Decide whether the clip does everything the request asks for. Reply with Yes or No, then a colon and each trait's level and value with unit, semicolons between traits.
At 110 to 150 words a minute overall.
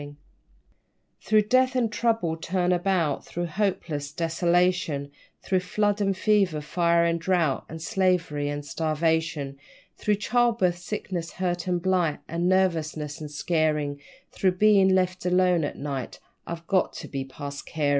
Yes: average, 145 wpm